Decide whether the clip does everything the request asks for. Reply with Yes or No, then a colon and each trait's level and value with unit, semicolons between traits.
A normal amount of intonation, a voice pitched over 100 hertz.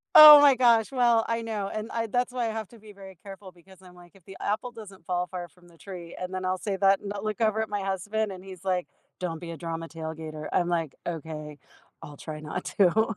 Yes: average, 4.0 semitones; high, 190 Hz